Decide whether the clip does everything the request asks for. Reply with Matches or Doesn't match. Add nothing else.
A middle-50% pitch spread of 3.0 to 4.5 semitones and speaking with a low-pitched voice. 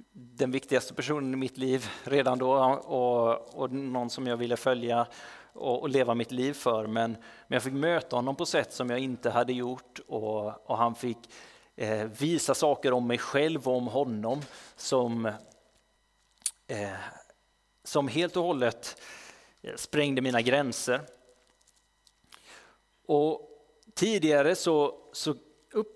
Matches